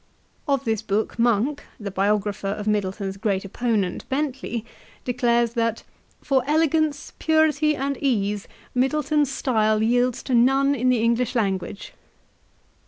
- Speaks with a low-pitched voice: No, high, 235 Hz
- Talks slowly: Yes, slow, 125 wpm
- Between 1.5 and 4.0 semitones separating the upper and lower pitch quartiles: No, average, 4.7 semitones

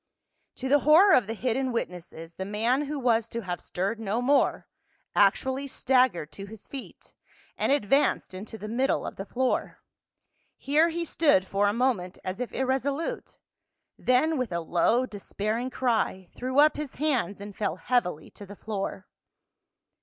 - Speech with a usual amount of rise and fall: Yes, average, 5.0 semitones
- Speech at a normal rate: Yes, average, 160 wpm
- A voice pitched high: Yes, high, 235 Hz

